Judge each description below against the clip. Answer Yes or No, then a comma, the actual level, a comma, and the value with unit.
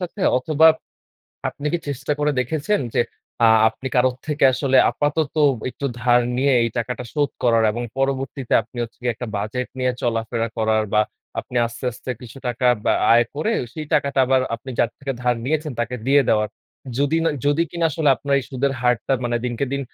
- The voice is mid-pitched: No, low, 130 Hz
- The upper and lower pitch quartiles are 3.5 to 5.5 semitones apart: No, average, 3.1 semitones